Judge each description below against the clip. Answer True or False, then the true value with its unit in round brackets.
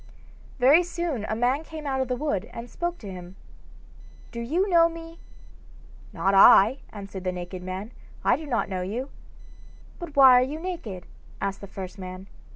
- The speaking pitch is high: True (240 Hz)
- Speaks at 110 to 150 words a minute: False (175 wpm)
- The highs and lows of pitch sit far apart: True (8.1 semitones)